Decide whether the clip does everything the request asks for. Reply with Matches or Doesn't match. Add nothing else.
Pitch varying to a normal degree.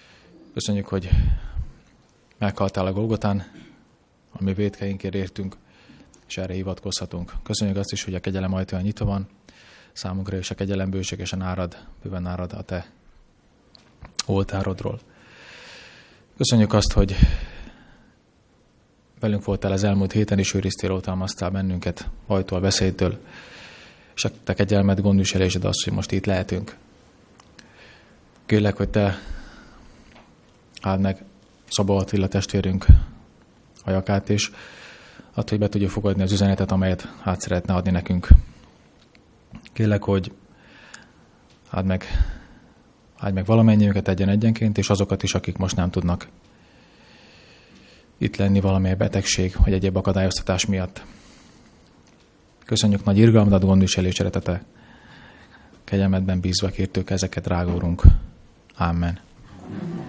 Doesn't match